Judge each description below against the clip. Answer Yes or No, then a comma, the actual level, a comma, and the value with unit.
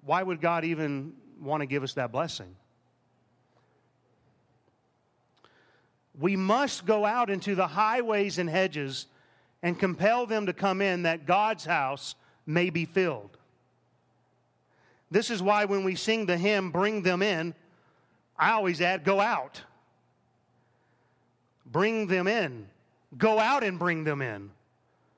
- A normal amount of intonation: No, wide, 6.8 semitones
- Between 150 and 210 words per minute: No, slow, 135 wpm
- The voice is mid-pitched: Yes, medium, 175 Hz